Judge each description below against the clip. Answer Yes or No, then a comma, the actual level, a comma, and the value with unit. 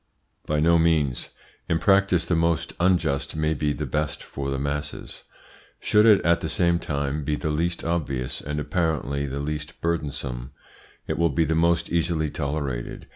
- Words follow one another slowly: No, average, 170 wpm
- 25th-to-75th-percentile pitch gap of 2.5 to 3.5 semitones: Yes, average, 3.0 semitones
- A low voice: Yes, very low, 75 Hz